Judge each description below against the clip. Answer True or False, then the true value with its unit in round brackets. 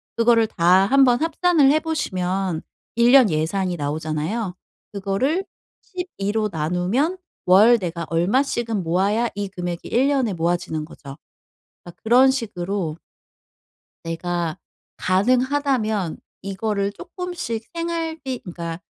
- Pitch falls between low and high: False (205 Hz)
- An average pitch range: False (6.9 semitones)